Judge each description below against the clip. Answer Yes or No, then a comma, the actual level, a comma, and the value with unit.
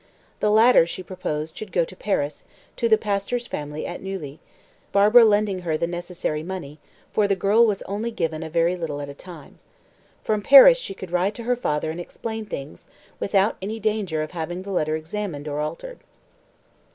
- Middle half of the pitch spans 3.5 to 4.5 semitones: No, average, 5.0 semitones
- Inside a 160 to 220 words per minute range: Yes, average, 190 wpm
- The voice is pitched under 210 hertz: Yes, medium, 185 Hz